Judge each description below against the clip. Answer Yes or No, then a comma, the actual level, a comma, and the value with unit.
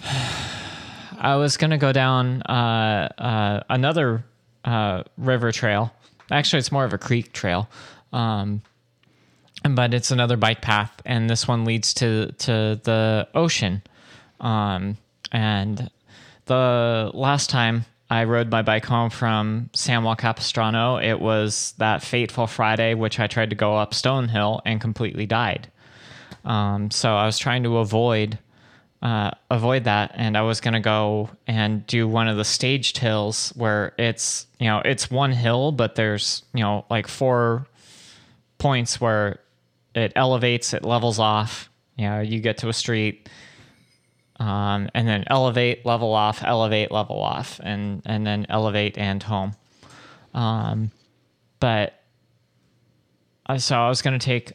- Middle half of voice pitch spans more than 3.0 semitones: No, narrow, 2.4 semitones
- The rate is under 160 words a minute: Yes, average, 150 wpm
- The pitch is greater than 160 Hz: No, low, 115 Hz